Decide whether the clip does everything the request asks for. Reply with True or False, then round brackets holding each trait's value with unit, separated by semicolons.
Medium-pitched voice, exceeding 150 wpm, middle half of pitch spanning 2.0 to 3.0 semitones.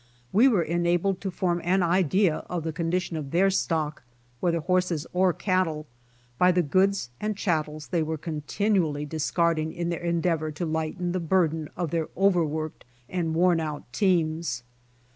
True (170 Hz; 160 wpm; 2.6 semitones)